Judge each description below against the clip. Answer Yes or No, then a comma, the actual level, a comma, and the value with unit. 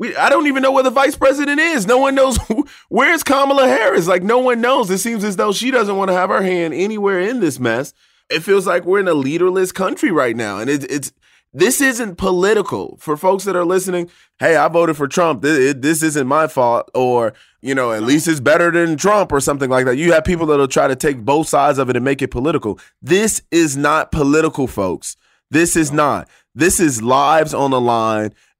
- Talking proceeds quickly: Yes, fast, 225 wpm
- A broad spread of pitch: Yes, wide, 7.7 semitones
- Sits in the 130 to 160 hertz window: No, medium, 170 Hz